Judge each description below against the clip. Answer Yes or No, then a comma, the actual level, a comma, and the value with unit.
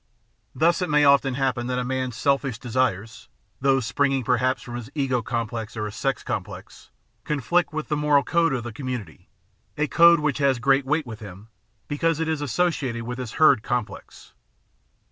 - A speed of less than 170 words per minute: No, average, 185 wpm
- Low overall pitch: Yes, low, 130 Hz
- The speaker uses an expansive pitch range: No, average, 3.6 semitones